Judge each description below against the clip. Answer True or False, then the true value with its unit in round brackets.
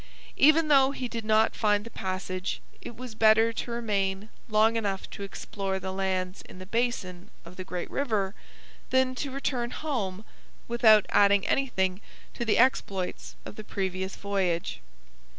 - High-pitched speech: True (210 Hz)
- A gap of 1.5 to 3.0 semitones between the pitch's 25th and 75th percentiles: False (3.8 semitones)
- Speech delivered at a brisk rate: False (155 wpm)